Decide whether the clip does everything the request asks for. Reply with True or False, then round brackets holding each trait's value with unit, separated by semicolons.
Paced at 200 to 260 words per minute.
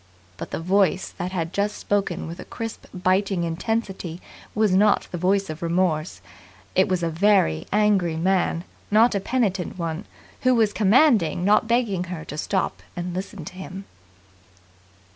False (160 wpm)